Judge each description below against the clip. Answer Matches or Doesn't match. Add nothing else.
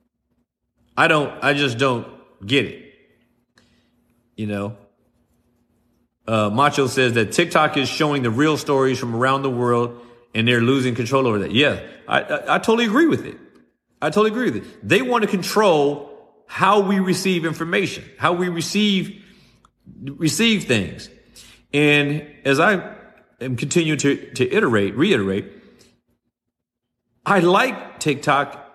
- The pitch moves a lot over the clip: Matches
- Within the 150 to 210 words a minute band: Doesn't match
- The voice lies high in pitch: Doesn't match